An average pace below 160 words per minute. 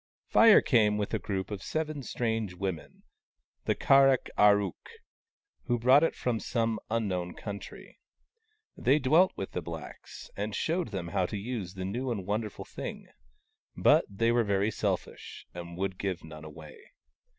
No: average, 165 wpm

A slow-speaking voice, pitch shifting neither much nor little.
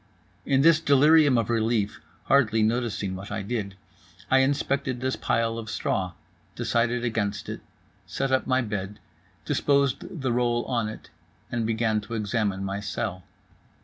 No: average, 145 wpm; average, 3.7 semitones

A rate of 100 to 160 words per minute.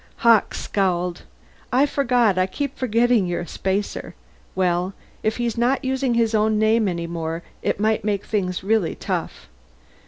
Yes: average, 155 wpm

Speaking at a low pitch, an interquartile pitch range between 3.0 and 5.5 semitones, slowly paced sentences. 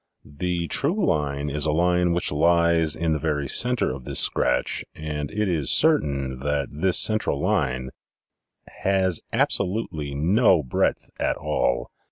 No: very low, 80 Hz; average, 4.2 semitones; average, 145 wpm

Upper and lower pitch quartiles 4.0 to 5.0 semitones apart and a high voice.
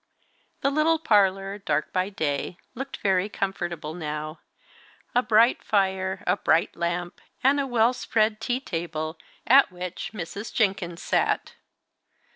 Yes: average, 4.7 semitones; high, 195 Hz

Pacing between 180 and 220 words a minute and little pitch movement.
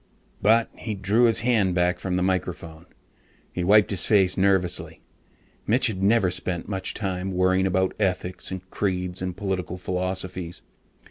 No: average, 155 wpm; narrow, 1.6 semitones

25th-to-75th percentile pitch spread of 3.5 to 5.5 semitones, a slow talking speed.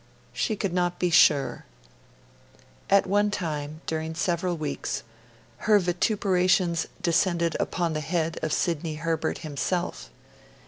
No: narrow, 2.6 semitones; slow, 120 wpm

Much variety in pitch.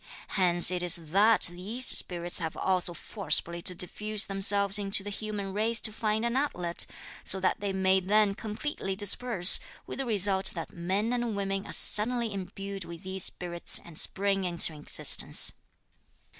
No: average, 3.0 semitones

